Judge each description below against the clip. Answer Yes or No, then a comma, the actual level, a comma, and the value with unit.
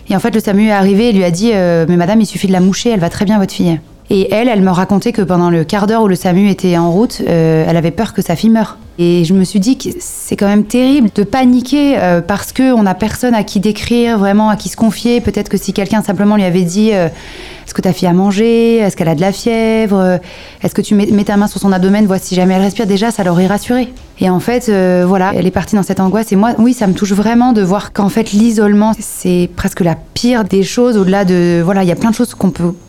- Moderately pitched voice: No, high, 200 Hz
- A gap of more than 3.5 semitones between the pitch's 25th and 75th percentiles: No, average, 3.0 semitones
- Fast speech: Yes, fast, 275 wpm